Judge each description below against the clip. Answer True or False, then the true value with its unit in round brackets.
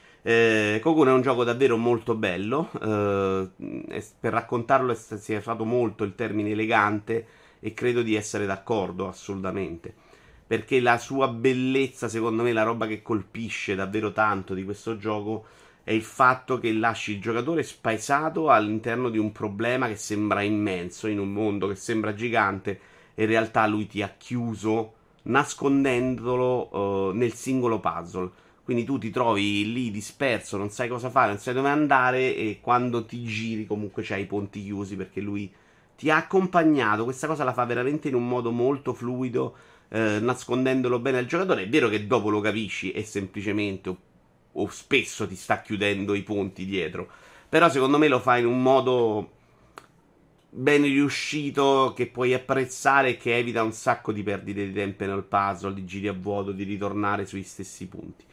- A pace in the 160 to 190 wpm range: True (170 wpm)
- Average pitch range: True (3.5 semitones)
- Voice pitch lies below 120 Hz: True (110 Hz)